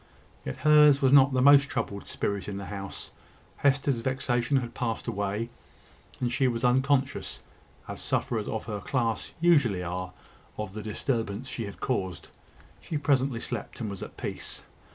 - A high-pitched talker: No, low, 120 Hz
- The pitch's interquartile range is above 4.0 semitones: Yes, average, 4.7 semitones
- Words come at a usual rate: Yes, average, 160 wpm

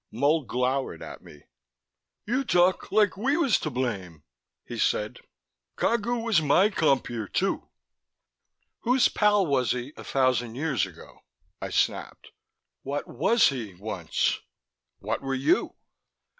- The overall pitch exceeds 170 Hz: No, medium, 140 Hz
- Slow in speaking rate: Yes, slow, 130 wpm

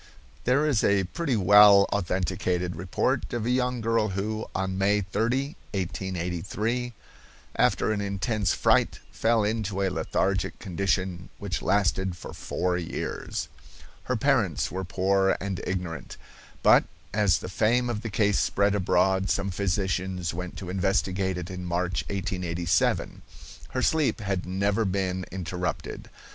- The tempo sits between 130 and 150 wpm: Yes, slow, 135 wpm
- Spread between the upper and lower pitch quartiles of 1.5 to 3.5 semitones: Yes, narrow, 2.6 semitones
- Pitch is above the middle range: No, very low, 95 Hz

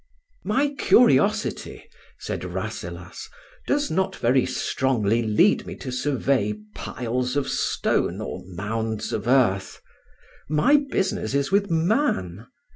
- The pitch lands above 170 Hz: No, low, 135 Hz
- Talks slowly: Yes, slow, 115 wpm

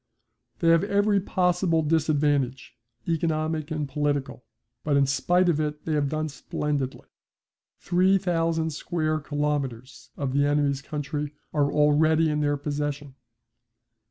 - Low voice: No, medium, 150 Hz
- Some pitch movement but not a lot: No, narrow, 2.2 semitones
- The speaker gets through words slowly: Yes, slow, 130 wpm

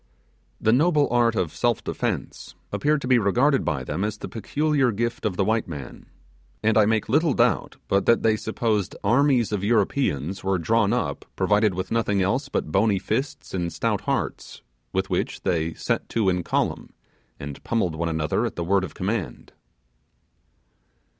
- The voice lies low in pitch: Yes, low, 105 Hz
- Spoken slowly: No, average, 170 wpm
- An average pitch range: Yes, average, 4.5 semitones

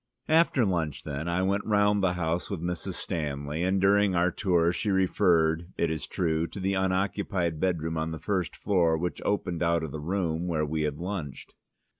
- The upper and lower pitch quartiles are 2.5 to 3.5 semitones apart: Yes, average, 2.9 semitones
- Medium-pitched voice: No, very low, 85 Hz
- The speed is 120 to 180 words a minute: No, average, 190 wpm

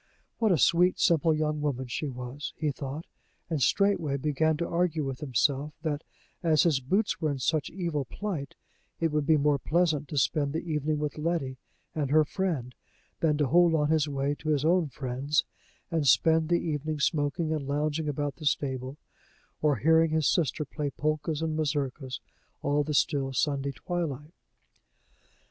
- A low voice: No, medium, 150 Hz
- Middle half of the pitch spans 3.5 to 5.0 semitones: No, narrow, 2.4 semitones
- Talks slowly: No, average, 170 wpm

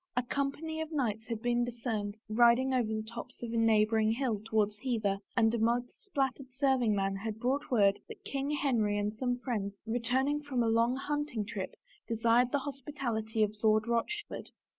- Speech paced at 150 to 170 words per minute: No, average, 185 wpm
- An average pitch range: Yes, average, 3.4 semitones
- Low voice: No, high, 235 Hz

